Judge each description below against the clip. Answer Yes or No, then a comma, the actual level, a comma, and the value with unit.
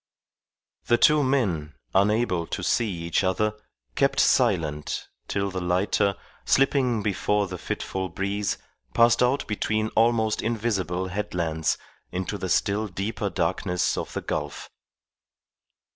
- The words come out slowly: Yes, slow, 120 wpm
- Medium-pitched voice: No, low, 100 Hz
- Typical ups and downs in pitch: Yes, average, 3.6 semitones